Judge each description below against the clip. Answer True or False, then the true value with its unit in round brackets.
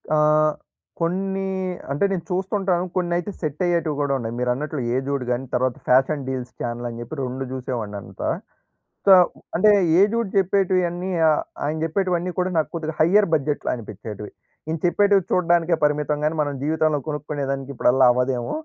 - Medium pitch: True (150 Hz)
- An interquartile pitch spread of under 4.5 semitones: False (5.2 semitones)